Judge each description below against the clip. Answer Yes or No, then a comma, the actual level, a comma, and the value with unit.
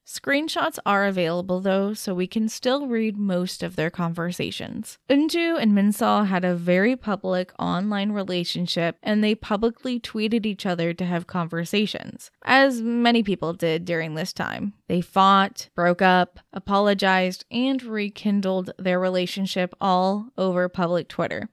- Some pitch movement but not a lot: Yes, average, 3.4 semitones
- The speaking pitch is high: Yes, high, 195 Hz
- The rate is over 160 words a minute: No, average, 140 wpm